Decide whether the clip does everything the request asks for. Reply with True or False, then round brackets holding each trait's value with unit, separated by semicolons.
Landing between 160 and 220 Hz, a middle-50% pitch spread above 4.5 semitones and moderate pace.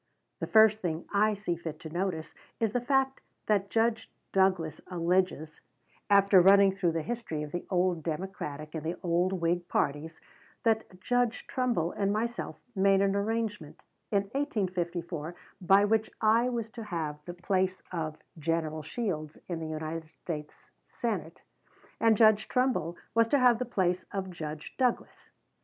True (185 Hz; 4.9 semitones; 155 wpm)